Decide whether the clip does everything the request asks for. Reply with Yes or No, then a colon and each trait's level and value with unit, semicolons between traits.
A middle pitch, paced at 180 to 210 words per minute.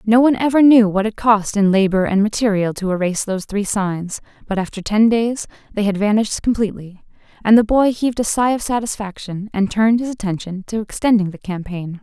No: high, 210 Hz; average, 200 wpm